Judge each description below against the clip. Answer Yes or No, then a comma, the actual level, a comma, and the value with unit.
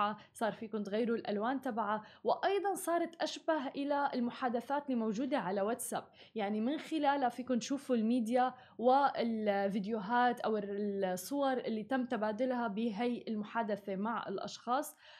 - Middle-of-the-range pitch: No, high, 240 Hz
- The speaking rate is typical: Yes, average, 115 wpm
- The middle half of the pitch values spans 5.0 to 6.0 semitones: No, average, 3.8 semitones